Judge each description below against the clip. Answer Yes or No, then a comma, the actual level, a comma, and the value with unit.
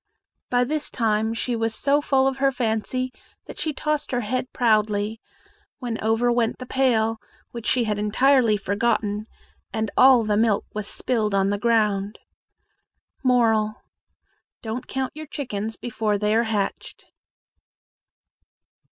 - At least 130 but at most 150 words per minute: Yes, average, 140 wpm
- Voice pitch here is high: Yes, high, 225 Hz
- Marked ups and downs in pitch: No, average, 3.1 semitones